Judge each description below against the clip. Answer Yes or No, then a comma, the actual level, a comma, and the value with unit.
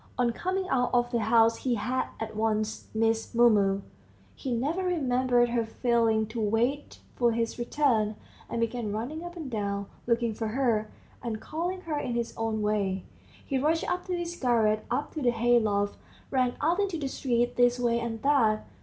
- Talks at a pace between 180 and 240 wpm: Yes, average, 185 wpm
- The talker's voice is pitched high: Yes, high, 240 Hz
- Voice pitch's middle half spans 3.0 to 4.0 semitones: Yes, average, 3.4 semitones